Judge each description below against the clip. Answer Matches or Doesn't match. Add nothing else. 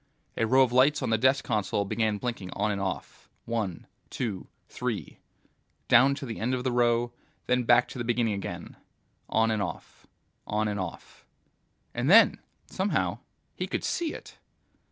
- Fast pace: Doesn't match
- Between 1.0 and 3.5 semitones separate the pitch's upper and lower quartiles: Matches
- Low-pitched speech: Matches